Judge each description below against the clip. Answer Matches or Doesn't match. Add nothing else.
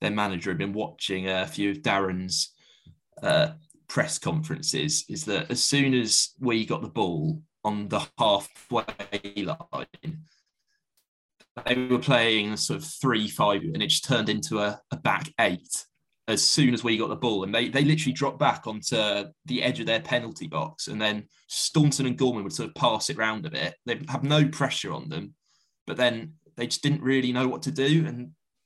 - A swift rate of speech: Doesn't match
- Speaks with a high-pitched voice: Doesn't match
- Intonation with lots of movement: Matches